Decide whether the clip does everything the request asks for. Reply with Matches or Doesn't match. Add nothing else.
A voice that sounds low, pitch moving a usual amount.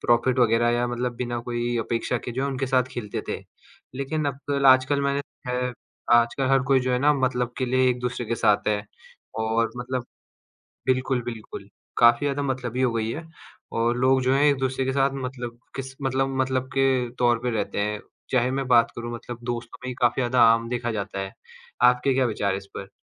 Doesn't match